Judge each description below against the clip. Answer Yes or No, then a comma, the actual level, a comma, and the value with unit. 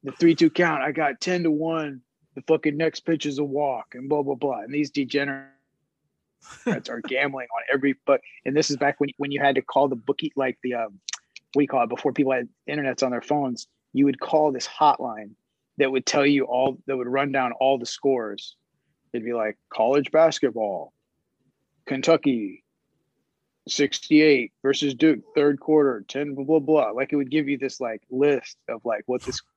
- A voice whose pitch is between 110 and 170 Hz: Yes, medium, 140 Hz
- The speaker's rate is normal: Yes, average, 195 wpm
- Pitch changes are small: Yes, narrow, 2.2 semitones